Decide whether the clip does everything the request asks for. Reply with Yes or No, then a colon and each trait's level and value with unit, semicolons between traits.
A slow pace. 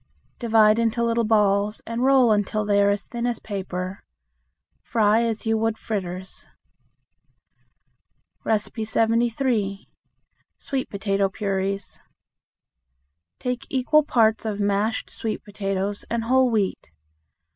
Yes: slow, 110 wpm